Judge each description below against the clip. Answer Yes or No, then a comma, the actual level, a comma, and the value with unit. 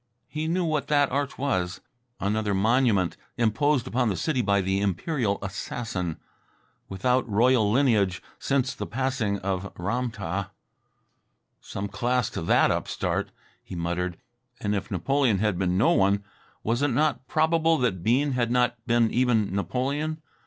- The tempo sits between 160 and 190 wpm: No, average, 145 wpm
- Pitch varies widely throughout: No, average, 5.0 semitones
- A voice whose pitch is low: Yes, low, 115 Hz